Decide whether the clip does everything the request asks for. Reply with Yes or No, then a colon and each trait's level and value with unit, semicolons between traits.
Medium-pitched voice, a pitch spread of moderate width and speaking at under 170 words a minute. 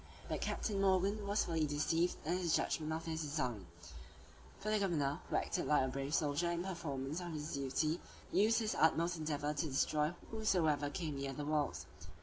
No: medium, 160 Hz; average, 3.4 semitones; average, 180 wpm